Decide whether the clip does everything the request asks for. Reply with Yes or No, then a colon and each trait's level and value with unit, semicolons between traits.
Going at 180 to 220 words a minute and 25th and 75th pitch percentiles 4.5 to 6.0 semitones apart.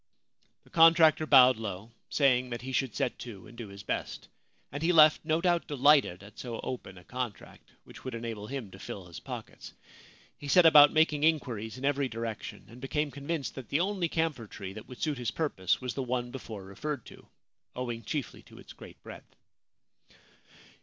Yes: average, 195 wpm; average, 5.0 semitones